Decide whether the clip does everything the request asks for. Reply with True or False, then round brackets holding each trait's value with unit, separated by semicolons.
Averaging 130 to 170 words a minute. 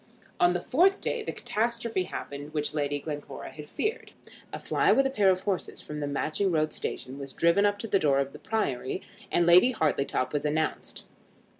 False (195 wpm)